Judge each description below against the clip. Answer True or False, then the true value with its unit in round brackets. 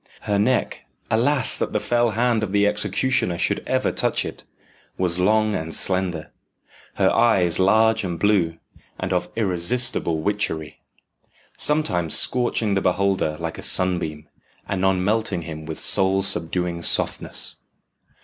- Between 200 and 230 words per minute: False (135 wpm)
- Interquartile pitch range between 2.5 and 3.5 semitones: False (4.0 semitones)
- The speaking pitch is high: False (95 Hz)